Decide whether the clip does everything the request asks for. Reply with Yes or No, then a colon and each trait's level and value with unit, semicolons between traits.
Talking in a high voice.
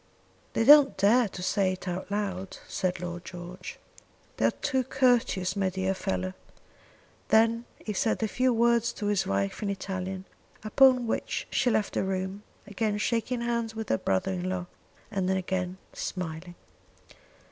Yes: high, 195 Hz